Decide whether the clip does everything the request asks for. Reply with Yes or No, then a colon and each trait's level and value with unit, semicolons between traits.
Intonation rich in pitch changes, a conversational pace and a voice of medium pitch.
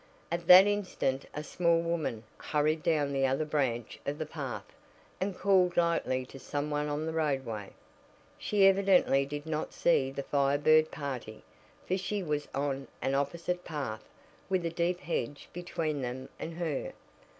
No: average, 3.8 semitones; average, 160 wpm; medium, 150 Hz